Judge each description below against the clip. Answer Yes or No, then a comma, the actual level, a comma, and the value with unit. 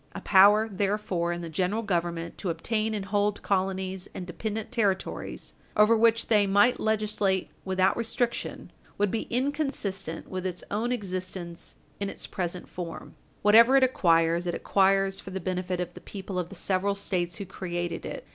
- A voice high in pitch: Yes, high, 195 Hz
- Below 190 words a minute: Yes, average, 165 wpm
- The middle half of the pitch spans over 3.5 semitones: No, average, 2.9 semitones